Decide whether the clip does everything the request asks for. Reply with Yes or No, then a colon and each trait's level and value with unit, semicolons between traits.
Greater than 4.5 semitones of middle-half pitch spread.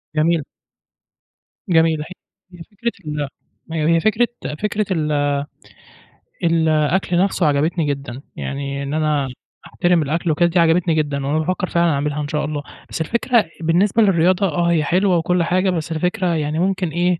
No: average, 3.0 semitones